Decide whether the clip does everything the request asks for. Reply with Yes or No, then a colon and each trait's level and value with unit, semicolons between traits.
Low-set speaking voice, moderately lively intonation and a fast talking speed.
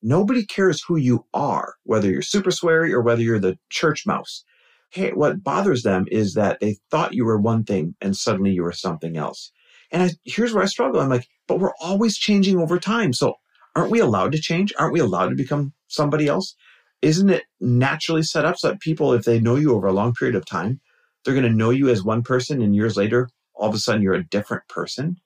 No: low, 125 Hz; wide, 7.5 semitones; fast, 230 wpm